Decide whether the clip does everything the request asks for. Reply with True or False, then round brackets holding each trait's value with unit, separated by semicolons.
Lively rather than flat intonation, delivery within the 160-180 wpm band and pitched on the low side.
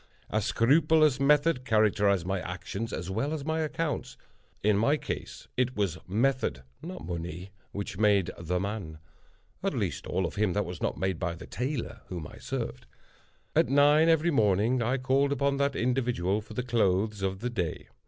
True (6.4 semitones; 170 wpm; 110 Hz)